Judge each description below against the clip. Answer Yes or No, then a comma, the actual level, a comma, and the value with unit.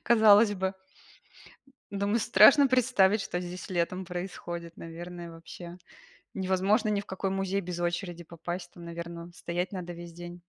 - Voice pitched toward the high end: No, medium, 180 Hz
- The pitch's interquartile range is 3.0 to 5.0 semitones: No, narrow, 2.4 semitones